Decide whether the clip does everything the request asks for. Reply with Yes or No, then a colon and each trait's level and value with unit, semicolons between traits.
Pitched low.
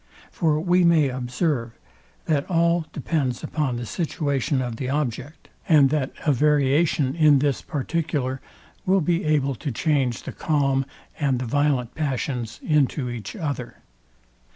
No: medium, 145 Hz